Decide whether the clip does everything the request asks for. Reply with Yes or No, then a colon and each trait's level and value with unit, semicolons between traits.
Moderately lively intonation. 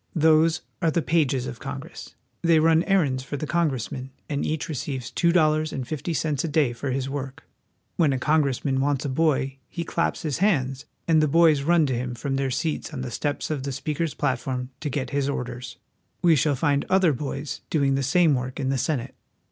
Yes: average, 3.2 semitones